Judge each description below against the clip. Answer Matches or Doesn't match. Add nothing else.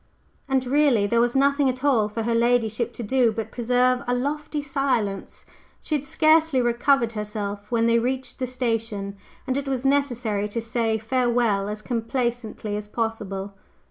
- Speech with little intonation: Doesn't match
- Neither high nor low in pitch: Doesn't match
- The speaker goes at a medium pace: Matches